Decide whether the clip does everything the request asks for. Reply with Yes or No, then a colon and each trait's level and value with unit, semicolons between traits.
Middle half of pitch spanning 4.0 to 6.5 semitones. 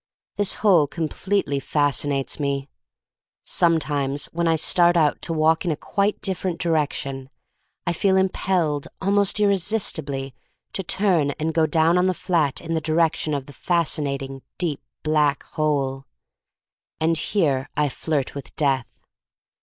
No: average, 3.6 semitones